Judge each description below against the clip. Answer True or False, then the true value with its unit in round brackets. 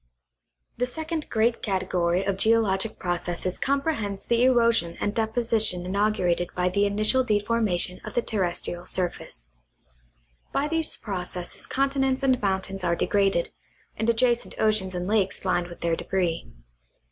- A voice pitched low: False (200 Hz)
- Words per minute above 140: False (135 wpm)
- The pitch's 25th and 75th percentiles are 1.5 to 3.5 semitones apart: False (4.5 semitones)